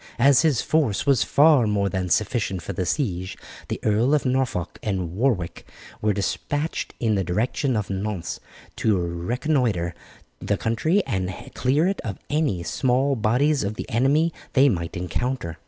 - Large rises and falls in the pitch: Yes, wide, 6.3 semitones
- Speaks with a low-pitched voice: Yes, low, 115 Hz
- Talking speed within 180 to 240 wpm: No, average, 155 wpm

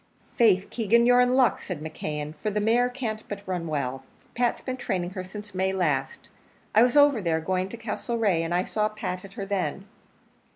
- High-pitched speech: Yes, high, 200 Hz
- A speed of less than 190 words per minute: No, average, 200 wpm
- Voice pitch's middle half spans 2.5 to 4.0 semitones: No, average, 4.5 semitones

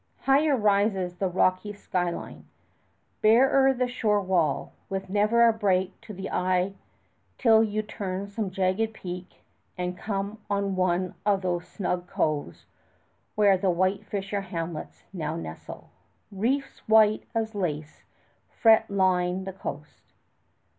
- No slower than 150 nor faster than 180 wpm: No, slow, 135 wpm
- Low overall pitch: No, high, 195 Hz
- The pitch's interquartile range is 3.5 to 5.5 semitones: No, average, 2.9 semitones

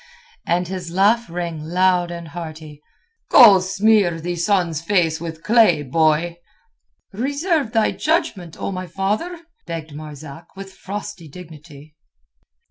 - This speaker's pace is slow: Yes, slow, 125 wpm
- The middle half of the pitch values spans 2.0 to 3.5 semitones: No, average, 3.9 semitones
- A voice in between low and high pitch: Yes, medium, 175 Hz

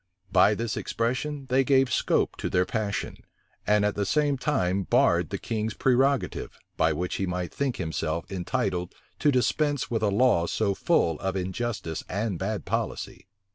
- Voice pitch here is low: Yes, low, 105 Hz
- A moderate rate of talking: Yes, average, 165 wpm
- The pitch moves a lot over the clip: Yes, wide, 5.8 semitones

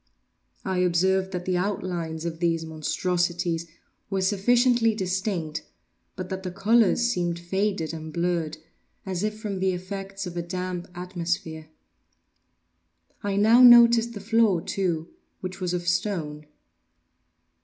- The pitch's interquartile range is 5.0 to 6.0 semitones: No, narrow, 2.6 semitones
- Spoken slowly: Yes, slow, 130 wpm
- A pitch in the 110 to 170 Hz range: No, medium, 185 Hz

